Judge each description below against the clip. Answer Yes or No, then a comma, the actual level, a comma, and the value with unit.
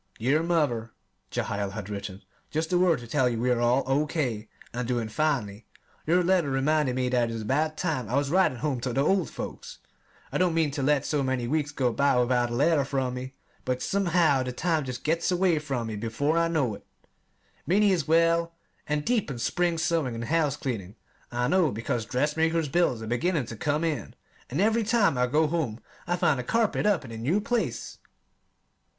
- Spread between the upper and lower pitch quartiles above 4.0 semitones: Yes, average, 5.2 semitones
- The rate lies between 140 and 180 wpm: No, fast, 205 wpm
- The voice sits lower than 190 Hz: Yes, medium, 140 Hz